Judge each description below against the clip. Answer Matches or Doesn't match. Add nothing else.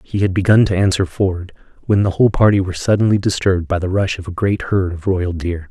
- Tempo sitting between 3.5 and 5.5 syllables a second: Doesn't match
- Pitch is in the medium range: Doesn't match